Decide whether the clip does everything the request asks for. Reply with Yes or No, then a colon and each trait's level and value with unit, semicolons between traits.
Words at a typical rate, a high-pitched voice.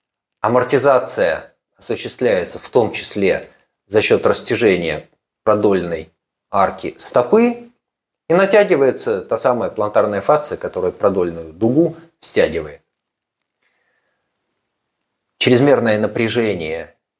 No: slow, 80 wpm; high, 235 Hz